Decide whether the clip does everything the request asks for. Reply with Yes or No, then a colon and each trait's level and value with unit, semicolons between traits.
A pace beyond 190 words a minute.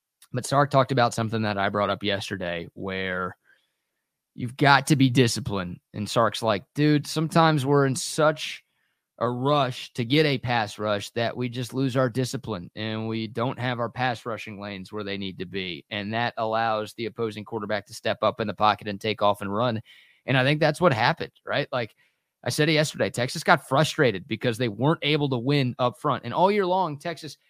Yes: fast, 205 wpm